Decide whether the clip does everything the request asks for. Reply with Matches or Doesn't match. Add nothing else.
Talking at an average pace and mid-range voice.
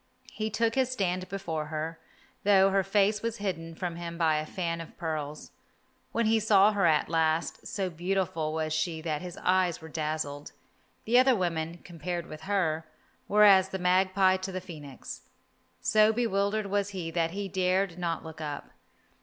Matches